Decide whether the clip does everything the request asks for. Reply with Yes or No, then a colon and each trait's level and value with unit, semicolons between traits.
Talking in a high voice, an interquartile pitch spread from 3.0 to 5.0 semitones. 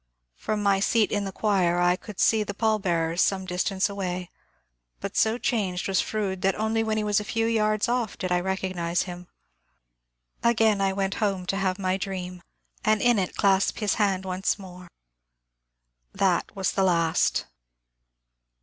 No: high, 195 Hz; narrow, 2.6 semitones